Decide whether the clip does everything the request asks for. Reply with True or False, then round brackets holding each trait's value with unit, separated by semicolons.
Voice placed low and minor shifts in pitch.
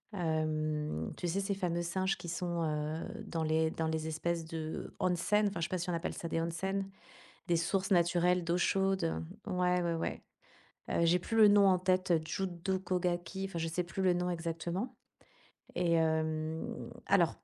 False (175 Hz; 2.2 semitones)